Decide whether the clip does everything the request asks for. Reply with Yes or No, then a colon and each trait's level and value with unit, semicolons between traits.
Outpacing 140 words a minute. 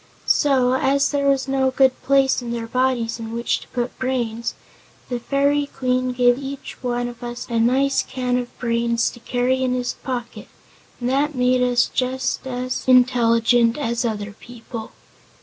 Yes: average, 165 wpm